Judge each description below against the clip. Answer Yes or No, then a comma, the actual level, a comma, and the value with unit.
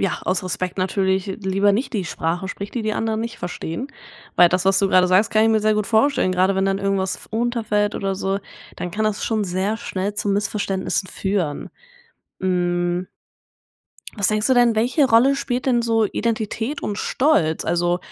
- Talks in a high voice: Yes, high, 200 Hz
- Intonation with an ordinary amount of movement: Yes, average, 3.1 semitones